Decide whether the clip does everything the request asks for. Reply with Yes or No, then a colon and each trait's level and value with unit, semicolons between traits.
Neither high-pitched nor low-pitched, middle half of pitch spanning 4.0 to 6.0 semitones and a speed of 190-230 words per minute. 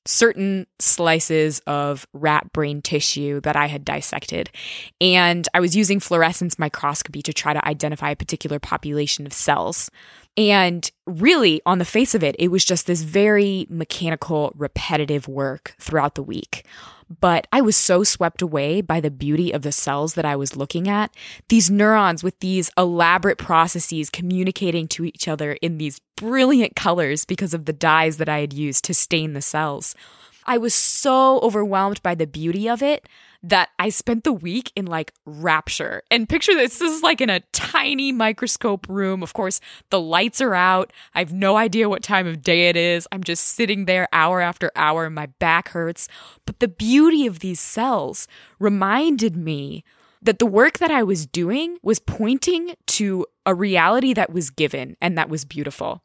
No: medium, 175 Hz; average, 5.1 semitones; average, 180 wpm